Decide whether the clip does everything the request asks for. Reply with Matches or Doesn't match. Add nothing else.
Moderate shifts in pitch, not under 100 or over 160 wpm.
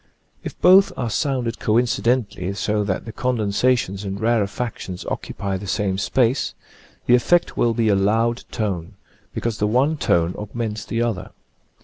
Matches